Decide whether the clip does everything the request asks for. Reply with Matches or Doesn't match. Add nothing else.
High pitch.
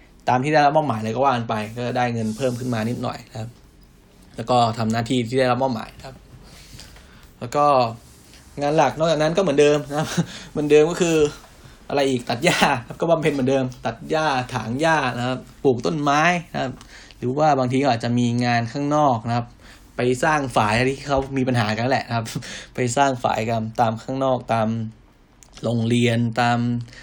Doesn't match